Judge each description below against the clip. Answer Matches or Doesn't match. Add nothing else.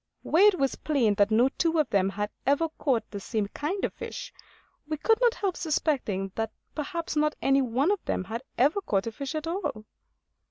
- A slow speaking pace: Doesn't match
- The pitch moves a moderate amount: Doesn't match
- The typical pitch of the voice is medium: Doesn't match